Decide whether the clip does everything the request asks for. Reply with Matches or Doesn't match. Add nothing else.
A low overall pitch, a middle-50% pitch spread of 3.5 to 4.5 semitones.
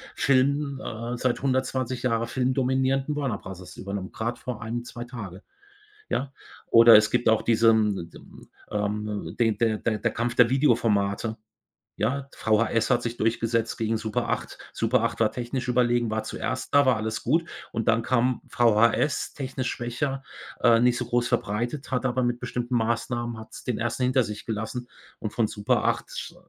Doesn't match